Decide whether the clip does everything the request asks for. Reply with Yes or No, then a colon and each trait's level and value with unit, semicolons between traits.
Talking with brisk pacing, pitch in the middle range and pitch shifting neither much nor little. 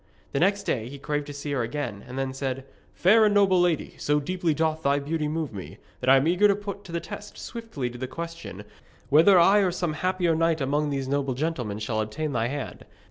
Yes: fast, 230 wpm; medium, 150 Hz; average, 4.7 semitones